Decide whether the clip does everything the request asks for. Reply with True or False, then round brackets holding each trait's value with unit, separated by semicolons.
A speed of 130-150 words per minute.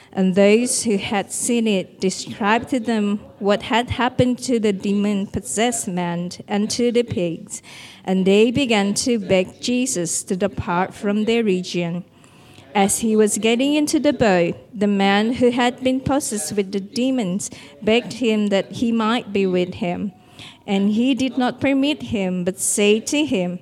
False (170 wpm)